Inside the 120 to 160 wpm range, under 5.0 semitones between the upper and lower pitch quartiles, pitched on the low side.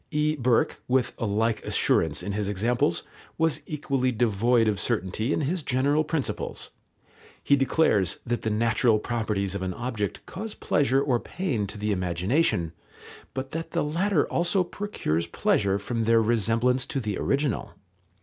No: average, 155 wpm; wide, 5.4 semitones; low, 120 Hz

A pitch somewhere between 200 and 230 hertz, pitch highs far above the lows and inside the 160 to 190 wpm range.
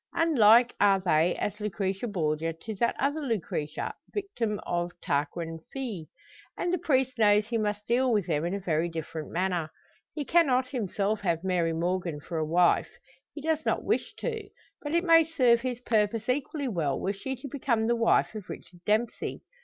Yes: high, 210 Hz; wide, 6.7 semitones; average, 180 wpm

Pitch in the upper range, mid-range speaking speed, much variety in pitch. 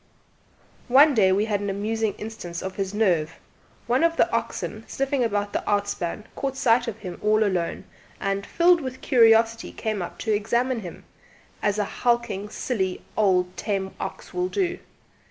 No: high, 215 Hz; average, 165 wpm; average, 3.8 semitones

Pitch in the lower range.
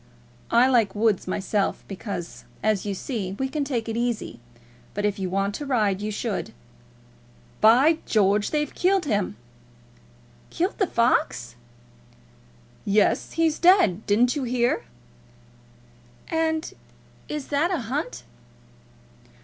No: high, 230 Hz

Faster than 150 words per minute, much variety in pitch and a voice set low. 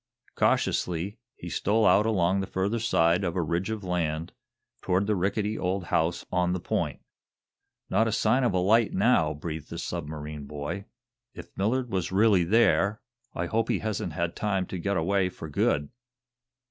No: average, 170 wpm; average, 3.9 semitones; very low, 95 Hz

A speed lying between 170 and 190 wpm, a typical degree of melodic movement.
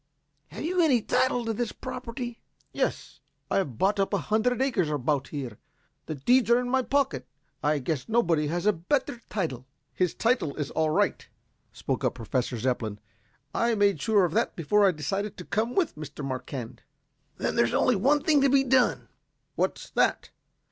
No: average, 180 wpm; wide, 8.8 semitones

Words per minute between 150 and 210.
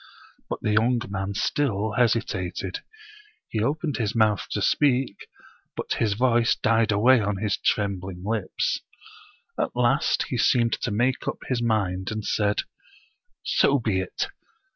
No: average, 140 wpm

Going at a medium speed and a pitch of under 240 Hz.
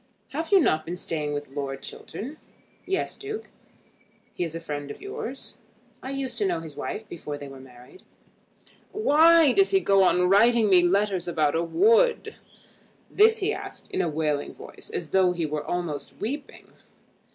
Yes: average, 175 wpm; medium, 185 Hz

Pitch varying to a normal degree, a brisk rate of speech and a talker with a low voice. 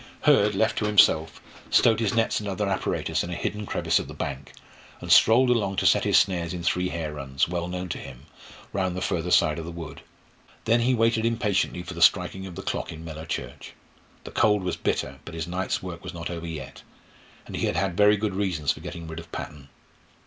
Yes: average, 3.9 semitones; fast, 225 wpm; very low, 90 Hz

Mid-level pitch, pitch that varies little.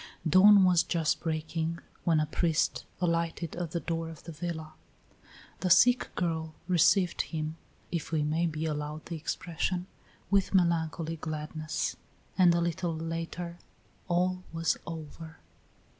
Yes: medium, 165 Hz; narrow, 1.7 semitones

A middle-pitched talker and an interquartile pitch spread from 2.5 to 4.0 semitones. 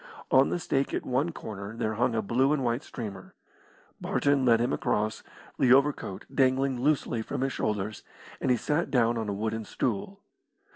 No: low, 120 Hz; average, 3.6 semitones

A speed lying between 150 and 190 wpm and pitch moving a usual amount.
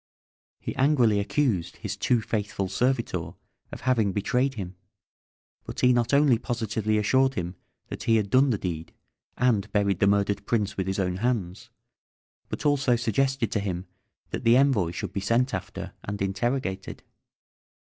Yes: average, 160 wpm; average, 4.4 semitones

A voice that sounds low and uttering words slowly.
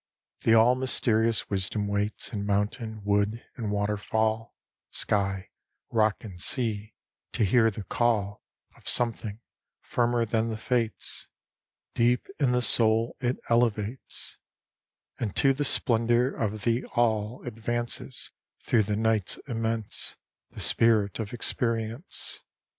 Yes: low, 110 Hz; slow, 120 wpm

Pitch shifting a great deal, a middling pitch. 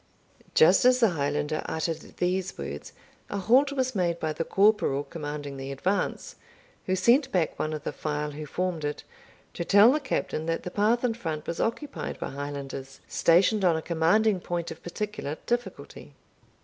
Yes: wide, 6.0 semitones; medium, 170 Hz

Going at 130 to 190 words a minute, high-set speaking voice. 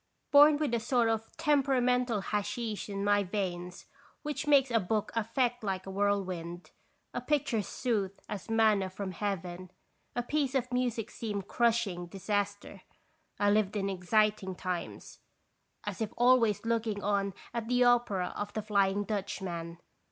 Yes: average, 150 wpm; high, 210 Hz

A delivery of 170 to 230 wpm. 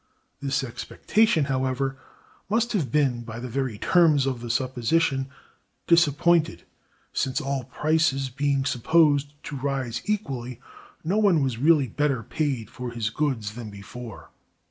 No: slow, 135 wpm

